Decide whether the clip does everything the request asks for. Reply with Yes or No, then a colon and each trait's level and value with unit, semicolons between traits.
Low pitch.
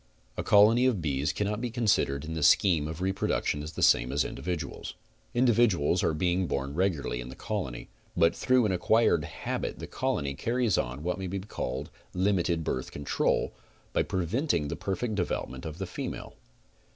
Yes: very low, 90 Hz